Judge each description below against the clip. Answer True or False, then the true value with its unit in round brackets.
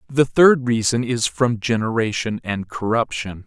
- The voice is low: True (115 Hz)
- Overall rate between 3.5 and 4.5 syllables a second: True (4.3 syllables/s)